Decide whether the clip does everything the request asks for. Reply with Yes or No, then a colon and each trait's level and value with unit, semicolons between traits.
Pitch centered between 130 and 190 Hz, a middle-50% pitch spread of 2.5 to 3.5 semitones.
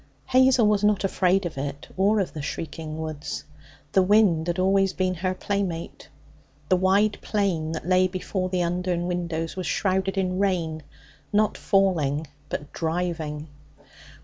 Yes: medium, 185 Hz; average, 3.1 semitones